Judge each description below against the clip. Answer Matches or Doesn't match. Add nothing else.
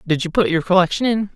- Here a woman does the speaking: Matches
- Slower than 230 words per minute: Doesn't match